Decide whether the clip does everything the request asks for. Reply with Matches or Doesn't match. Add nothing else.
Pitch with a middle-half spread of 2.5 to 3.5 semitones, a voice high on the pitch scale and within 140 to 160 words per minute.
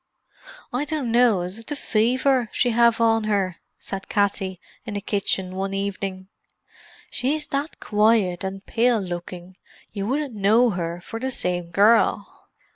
Doesn't match